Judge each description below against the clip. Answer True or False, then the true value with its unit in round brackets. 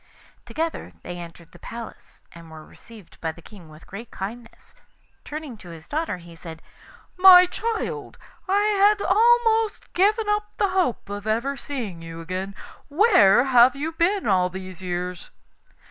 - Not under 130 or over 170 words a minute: True (155 wpm)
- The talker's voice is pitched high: True (230 Hz)